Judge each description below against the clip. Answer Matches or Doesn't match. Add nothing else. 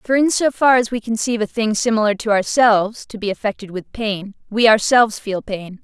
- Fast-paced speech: Matches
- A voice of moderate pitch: Doesn't match